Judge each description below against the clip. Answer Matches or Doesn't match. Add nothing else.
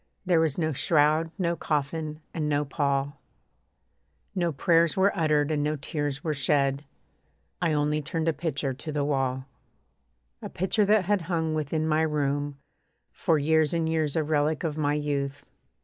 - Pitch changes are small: Matches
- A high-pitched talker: Doesn't match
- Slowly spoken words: Doesn't match